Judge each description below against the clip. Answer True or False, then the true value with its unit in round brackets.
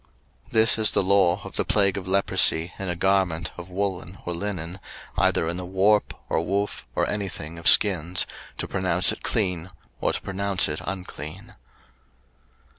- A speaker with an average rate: True (175 wpm)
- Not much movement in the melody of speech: True (2.2 semitones)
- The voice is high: False (95 Hz)